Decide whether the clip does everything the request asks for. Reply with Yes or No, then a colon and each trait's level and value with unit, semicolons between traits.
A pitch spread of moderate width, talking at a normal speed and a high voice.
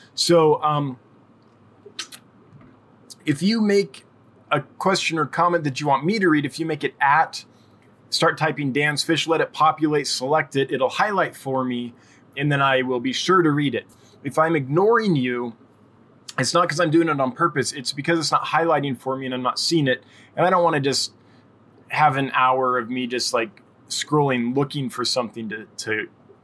No: average, 3.9 semitones; average, 195 wpm; medium, 140 Hz